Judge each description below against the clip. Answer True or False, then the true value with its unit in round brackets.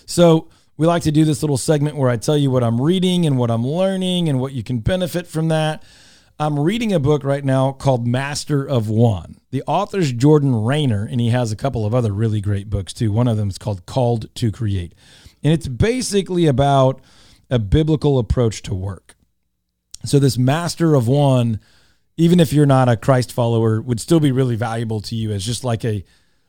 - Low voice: True (130 Hz)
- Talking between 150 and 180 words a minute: False (205 wpm)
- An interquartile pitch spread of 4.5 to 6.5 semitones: True (5.0 semitones)